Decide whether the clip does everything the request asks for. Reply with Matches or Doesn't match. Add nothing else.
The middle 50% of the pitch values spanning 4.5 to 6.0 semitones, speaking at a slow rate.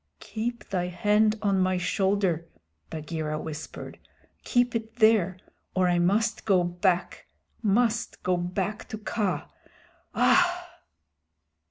Doesn't match